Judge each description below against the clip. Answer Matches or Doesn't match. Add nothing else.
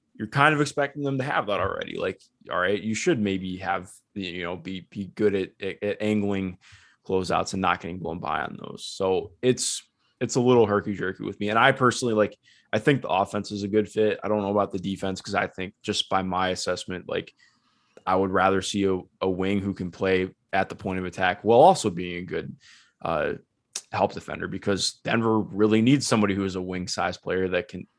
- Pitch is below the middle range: Matches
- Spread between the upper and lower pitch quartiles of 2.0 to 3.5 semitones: Matches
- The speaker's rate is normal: Doesn't match